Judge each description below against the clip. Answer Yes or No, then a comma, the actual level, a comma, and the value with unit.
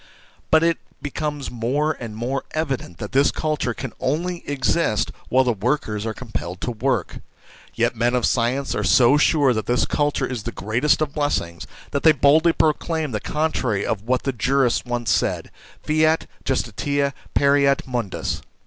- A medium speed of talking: Yes, average, 165 wpm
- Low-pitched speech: Yes, low, 130 Hz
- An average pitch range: Yes, average, 4.1 semitones